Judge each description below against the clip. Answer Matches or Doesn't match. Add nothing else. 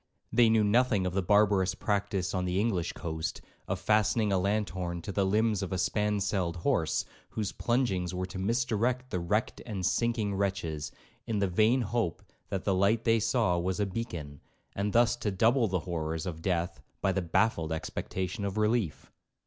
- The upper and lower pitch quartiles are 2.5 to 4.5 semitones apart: Matches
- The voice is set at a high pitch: Doesn't match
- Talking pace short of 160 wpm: Doesn't match